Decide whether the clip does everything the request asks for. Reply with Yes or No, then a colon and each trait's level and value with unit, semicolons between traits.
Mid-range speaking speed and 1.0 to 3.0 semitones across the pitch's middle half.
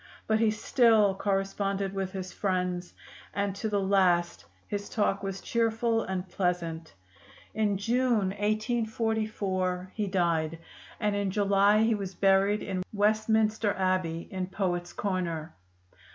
No: slow, 125 wpm; narrow, 2.5 semitones